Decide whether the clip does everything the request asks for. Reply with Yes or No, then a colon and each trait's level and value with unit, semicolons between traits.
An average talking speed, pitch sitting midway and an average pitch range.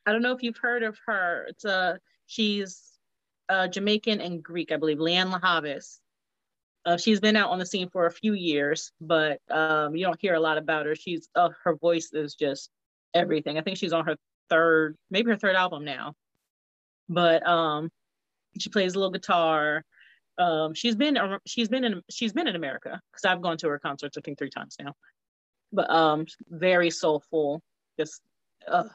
Yes: average, 190 wpm; medium, 170 Hz; average, 4.0 semitones